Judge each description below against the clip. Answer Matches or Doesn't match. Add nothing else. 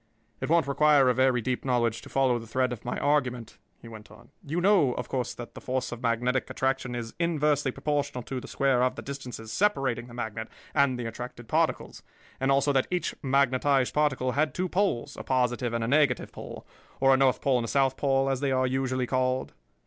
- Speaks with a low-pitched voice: Matches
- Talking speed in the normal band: Doesn't match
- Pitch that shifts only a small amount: Matches